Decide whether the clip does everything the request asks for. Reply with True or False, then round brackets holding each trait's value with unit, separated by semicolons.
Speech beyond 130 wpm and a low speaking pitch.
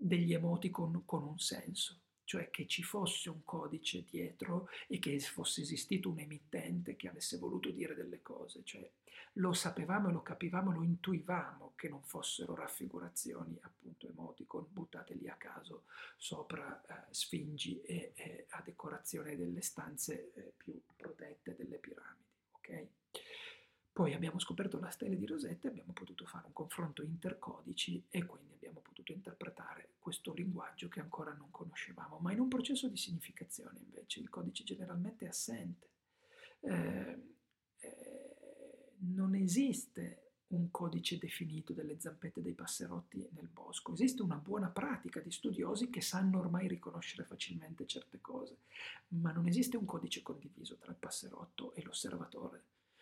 False (145 wpm; 175 Hz)